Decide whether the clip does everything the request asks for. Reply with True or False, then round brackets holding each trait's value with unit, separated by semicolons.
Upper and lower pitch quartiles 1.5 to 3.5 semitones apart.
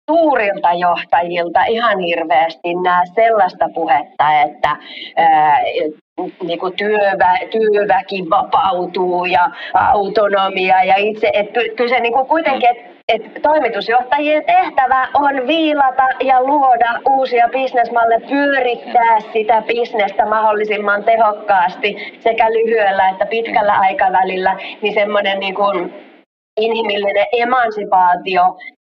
False (4.4 semitones)